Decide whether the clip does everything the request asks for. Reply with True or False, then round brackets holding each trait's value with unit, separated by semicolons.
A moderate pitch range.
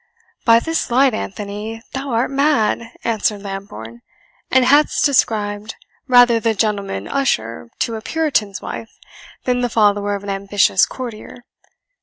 True (3.6 semitones)